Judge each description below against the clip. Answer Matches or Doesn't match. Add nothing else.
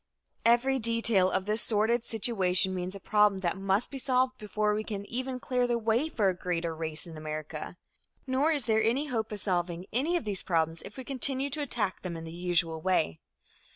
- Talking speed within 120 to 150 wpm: Doesn't match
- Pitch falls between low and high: Doesn't match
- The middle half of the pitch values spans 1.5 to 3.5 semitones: Doesn't match